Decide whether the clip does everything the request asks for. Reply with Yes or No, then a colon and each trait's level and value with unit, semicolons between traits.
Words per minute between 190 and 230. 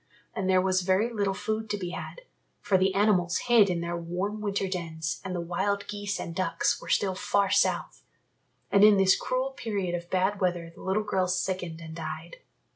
Yes: average, 200 wpm